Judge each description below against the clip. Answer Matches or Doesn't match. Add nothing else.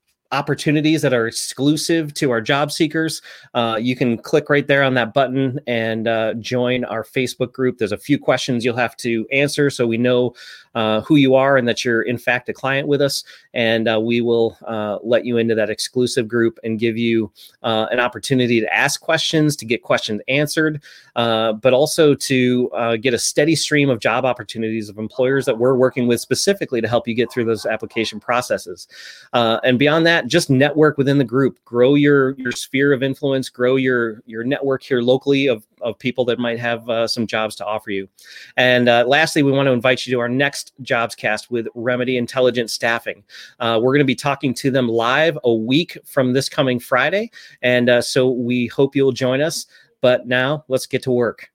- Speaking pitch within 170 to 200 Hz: Doesn't match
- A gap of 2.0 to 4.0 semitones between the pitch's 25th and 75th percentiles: Matches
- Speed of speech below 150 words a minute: Doesn't match